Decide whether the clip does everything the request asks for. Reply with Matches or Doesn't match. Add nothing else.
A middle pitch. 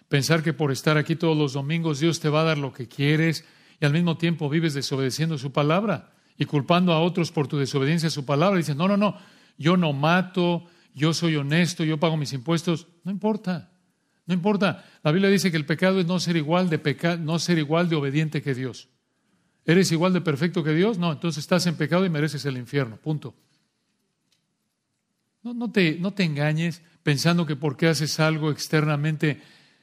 Matches